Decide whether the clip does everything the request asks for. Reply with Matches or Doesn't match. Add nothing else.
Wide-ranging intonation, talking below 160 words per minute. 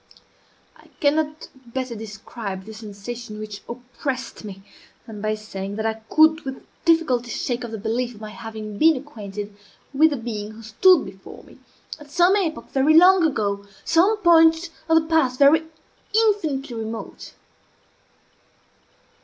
Matches